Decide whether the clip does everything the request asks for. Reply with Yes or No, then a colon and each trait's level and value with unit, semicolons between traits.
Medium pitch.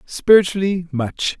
Yes: medium, 175 Hz